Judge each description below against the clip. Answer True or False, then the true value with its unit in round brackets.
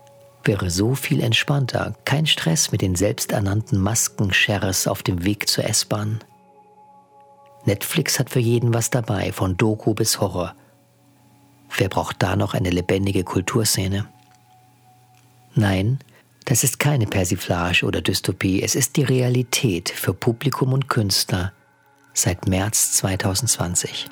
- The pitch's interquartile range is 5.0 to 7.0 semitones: True (5.4 semitones)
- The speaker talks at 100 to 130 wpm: True (125 wpm)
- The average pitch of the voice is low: True (115 Hz)